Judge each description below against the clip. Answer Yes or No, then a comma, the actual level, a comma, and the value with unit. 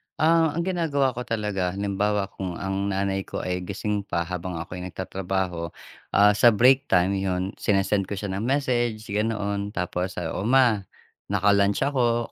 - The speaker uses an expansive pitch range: No, average, 3.6 semitones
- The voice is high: No, low, 100 Hz